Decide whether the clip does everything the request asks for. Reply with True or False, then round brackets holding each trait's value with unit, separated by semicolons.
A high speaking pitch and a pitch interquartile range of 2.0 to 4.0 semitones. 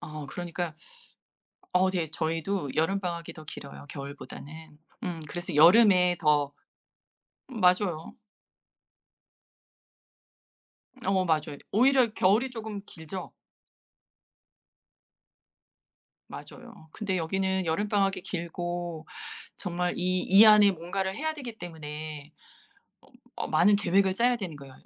False (180 Hz; 3.7 semitones)